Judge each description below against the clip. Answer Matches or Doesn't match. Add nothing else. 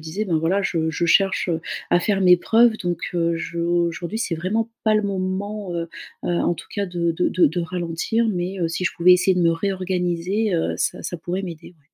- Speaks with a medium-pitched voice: Matches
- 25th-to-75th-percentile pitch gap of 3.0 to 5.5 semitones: Doesn't match